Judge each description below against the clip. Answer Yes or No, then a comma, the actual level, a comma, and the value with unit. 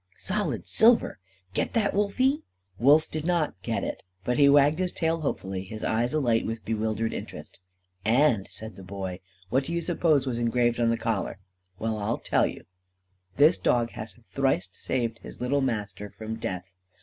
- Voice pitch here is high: No, low, 120 Hz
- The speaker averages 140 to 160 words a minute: No, average, 175 wpm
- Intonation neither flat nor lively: No, wide, 5.8 semitones